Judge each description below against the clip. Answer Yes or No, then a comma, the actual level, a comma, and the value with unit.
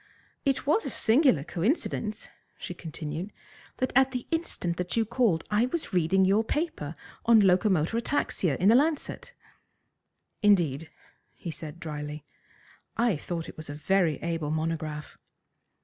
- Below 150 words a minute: Yes, average, 140 wpm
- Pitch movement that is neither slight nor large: No, wide, 6.8 semitones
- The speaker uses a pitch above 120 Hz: Yes, medium, 185 Hz